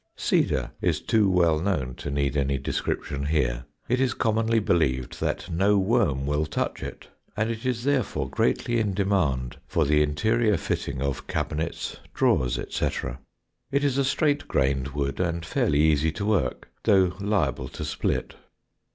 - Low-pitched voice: Yes, very low, 85 Hz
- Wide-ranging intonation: Yes, wide, 7.6 semitones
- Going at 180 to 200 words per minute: No, average, 160 wpm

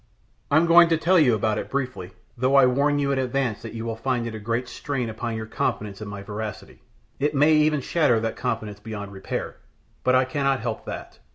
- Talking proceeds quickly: Yes, fast, 215 wpm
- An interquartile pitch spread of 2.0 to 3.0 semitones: No, average, 4.1 semitones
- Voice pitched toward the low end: Yes, low, 125 Hz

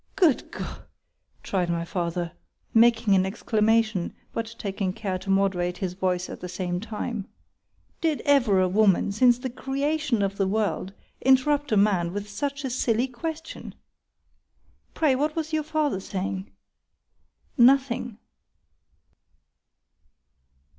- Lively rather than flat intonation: Yes, wide, 5.9 semitones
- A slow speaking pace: Yes, slow, 120 wpm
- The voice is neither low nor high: No, high, 215 Hz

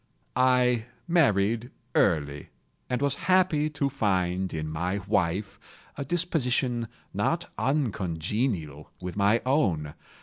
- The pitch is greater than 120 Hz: No, low, 115 Hz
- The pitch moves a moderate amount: No, wide, 7.1 semitones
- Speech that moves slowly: Yes, slow, 105 wpm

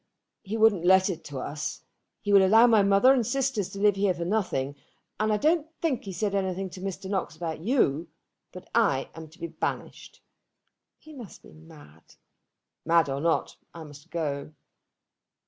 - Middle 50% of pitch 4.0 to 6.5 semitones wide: Yes, average, 4.8 semitones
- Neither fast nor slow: Yes, average, 180 wpm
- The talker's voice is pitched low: No, high, 190 Hz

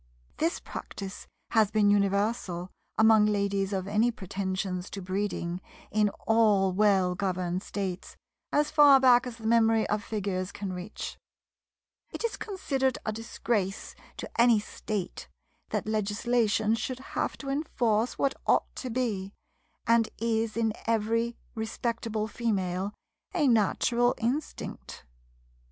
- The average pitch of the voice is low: No, high, 215 Hz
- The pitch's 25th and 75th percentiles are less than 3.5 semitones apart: Yes, average, 3.0 semitones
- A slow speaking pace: Yes, slow, 125 wpm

